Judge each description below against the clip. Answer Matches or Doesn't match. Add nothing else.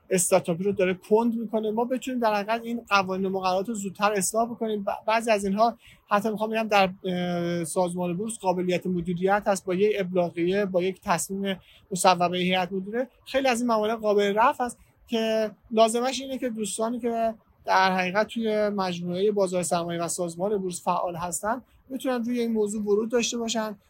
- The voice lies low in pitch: Doesn't match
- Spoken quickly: Matches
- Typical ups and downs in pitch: Matches